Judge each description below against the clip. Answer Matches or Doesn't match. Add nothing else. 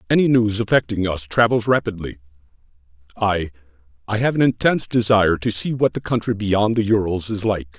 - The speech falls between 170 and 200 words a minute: Doesn't match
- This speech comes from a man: Matches